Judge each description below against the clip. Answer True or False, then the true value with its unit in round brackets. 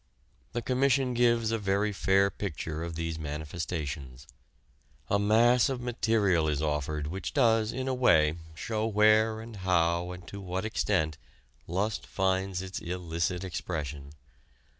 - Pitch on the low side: True (95 Hz)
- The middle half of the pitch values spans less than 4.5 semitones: False (5.4 semitones)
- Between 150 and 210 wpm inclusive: False (140 wpm)